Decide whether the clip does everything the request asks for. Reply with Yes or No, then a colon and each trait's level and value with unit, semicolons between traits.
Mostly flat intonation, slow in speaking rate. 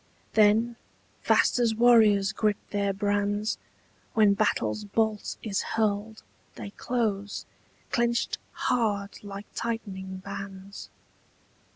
Yes: narrow, 2.0 semitones; slow, 95 wpm